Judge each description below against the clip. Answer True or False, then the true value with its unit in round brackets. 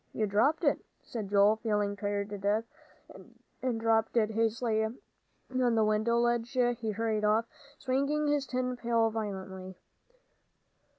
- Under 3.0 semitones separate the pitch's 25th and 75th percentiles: True (2.5 semitones)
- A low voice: False (225 Hz)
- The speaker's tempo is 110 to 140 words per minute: True (135 wpm)